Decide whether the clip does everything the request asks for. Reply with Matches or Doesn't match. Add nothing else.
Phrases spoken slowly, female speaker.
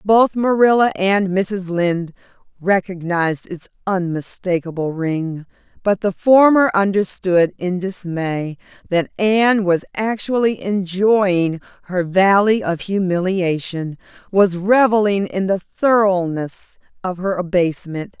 Matches